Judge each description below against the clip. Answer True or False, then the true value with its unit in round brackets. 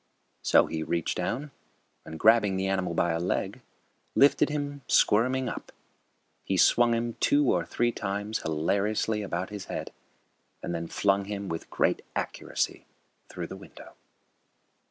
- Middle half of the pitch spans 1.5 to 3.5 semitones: False (5.1 semitones)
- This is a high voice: False (100 Hz)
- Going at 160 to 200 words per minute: False (145 wpm)